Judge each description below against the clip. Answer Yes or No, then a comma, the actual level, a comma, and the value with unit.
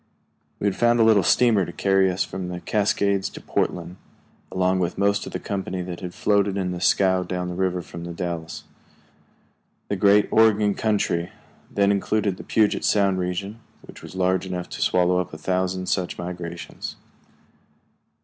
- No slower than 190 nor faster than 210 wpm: No, average, 170 wpm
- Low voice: Yes, very low, 95 Hz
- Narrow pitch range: Yes, narrow, 2.1 semitones